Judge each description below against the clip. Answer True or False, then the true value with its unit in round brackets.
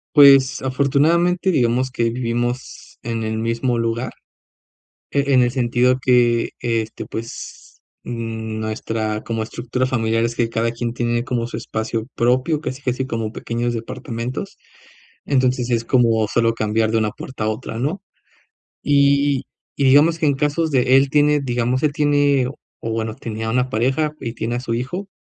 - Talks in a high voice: False (120 Hz)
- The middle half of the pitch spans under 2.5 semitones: False (2.9 semitones)